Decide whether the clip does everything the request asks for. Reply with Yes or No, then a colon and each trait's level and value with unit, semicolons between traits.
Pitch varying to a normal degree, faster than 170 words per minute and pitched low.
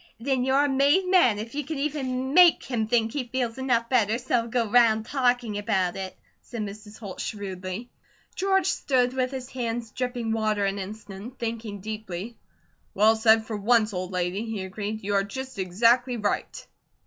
No: average, 3.6 semitones; average, 180 wpm; high, 230 Hz